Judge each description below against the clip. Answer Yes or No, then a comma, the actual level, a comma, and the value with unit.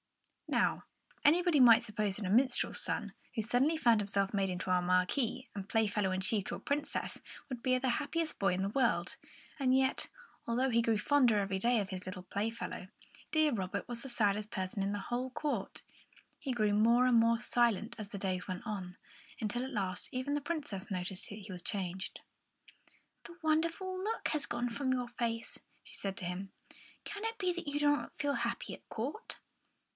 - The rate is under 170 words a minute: No, average, 195 wpm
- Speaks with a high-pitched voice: Yes, high, 230 Hz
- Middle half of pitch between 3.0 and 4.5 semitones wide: No, wide, 5.4 semitones